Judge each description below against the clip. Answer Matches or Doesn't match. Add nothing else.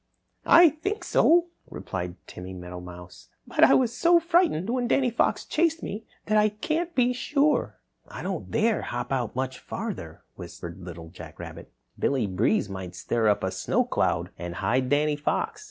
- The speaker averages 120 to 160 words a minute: Doesn't match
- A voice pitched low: Doesn't match